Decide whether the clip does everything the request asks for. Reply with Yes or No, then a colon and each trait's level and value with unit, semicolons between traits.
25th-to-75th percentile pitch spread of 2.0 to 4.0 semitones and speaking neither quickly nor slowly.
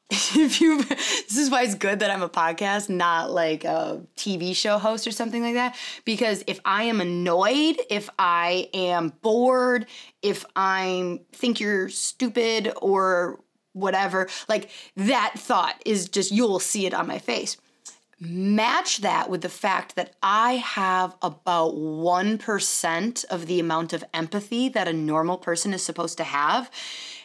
No: average, 4.8 semitones; average, 160 wpm